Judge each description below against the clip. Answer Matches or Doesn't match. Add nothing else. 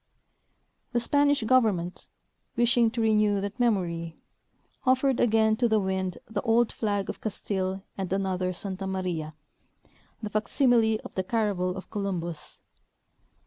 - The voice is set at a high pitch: Matches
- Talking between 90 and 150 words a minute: Matches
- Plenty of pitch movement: Doesn't match